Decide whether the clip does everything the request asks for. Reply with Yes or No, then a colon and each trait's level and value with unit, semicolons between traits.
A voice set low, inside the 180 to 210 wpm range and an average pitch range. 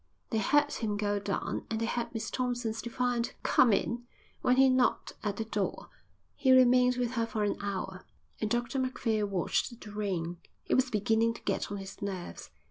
No: high, 225 Hz; average, 190 wpm; average, 3.4 semitones